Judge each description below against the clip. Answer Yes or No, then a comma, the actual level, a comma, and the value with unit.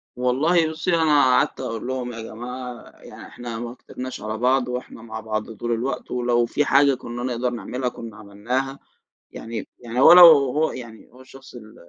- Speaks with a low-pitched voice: Yes, low, 125 Hz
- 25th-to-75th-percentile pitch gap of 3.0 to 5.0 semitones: No, narrow, 2.4 semitones